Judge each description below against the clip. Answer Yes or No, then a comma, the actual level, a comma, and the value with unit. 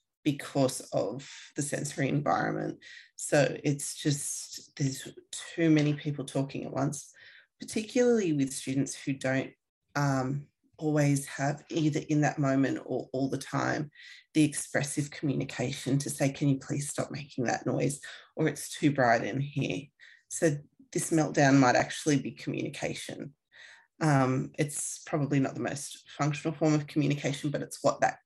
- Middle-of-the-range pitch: Yes, medium, 145 Hz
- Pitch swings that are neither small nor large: No, narrow, 2.0 semitones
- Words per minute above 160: No, average, 150 wpm